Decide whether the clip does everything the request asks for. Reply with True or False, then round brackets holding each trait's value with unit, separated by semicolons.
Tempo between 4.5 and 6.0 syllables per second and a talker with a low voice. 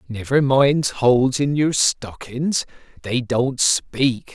False (3.2 syllables/s; 130 Hz)